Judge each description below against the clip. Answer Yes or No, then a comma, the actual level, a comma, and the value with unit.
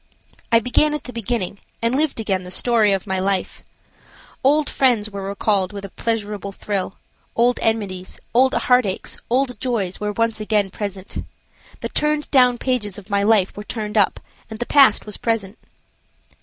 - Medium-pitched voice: No, high, 215 Hz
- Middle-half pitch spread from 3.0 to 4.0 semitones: Yes, average, 3.6 semitones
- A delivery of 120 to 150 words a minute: No, average, 170 wpm